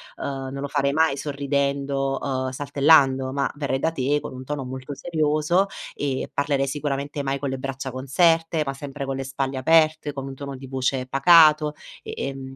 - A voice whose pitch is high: No, medium, 140 Hz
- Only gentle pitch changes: Yes, narrow, 1.6 semitones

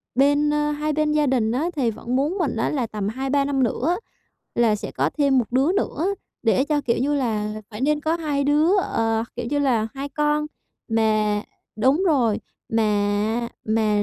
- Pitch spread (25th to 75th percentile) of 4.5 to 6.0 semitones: Yes, average, 5.1 semitones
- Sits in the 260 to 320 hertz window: Yes, very high, 265 Hz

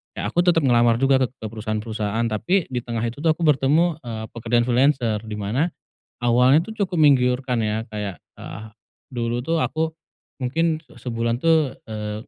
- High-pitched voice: No, low, 125 Hz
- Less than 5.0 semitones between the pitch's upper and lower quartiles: No, average, 5.3 semitones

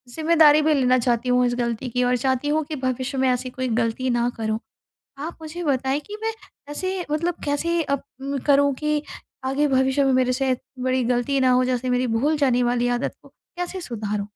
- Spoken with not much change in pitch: No, average, 3.0 semitones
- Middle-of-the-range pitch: No, very high, 260 Hz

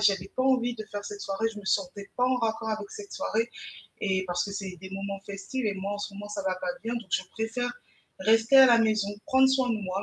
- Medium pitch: No, high, 205 Hz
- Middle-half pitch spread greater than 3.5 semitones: No, average, 2.8 semitones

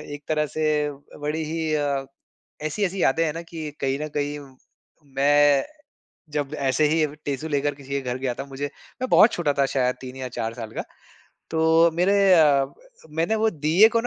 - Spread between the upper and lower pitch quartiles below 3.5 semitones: Yes, narrow, 2.6 semitones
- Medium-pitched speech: Yes, medium, 145 Hz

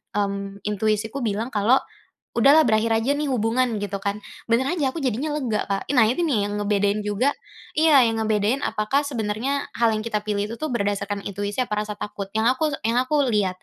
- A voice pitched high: Yes, high, 220 Hz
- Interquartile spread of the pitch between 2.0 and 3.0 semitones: No, average, 3.8 semitones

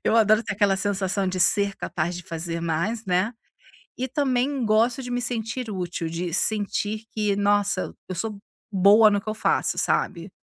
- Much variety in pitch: No, average, 3.3 semitones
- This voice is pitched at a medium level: No, high, 205 Hz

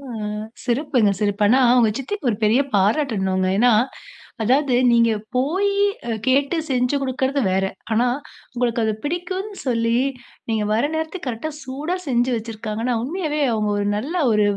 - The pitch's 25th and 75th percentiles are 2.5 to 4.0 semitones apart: No, average, 4.6 semitones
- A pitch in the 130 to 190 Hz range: No, high, 245 Hz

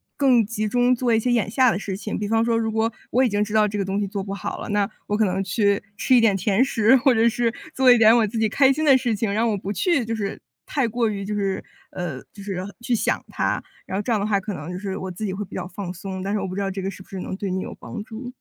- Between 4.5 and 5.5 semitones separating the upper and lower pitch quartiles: No, average, 2.9 semitones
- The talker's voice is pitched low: No, high, 210 Hz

